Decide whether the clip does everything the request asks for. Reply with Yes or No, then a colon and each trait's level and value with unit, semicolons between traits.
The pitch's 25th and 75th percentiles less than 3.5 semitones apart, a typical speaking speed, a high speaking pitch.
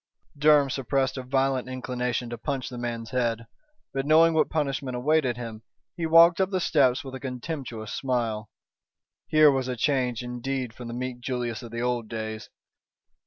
No: narrow, 2.5 semitones; average, 170 wpm; low, 130 Hz